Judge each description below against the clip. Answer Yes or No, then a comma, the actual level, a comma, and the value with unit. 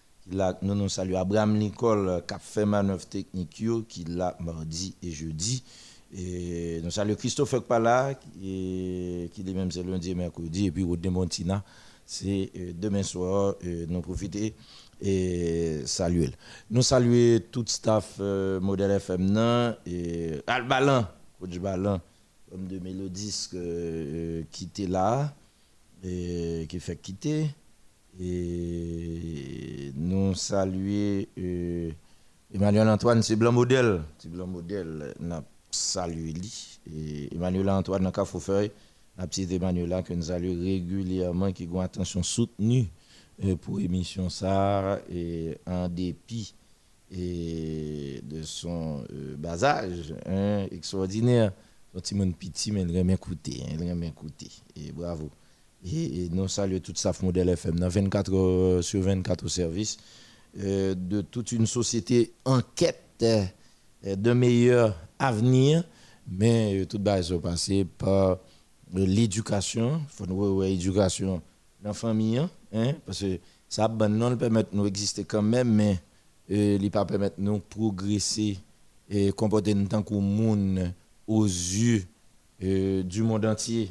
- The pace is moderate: No, slow, 135 wpm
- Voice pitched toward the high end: No, very low, 95 Hz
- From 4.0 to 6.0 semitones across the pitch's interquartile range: No, average, 3.2 semitones